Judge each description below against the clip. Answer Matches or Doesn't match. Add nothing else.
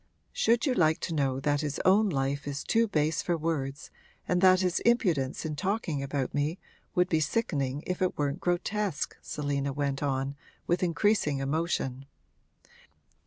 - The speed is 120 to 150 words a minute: Doesn't match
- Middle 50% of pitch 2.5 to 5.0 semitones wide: Matches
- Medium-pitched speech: Matches